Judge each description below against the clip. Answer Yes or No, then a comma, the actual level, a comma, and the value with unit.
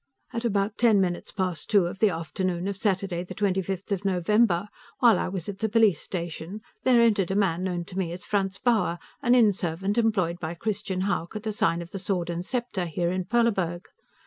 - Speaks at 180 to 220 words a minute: Yes, average, 200 wpm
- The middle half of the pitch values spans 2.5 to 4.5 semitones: Yes, average, 3.3 semitones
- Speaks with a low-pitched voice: No, high, 195 Hz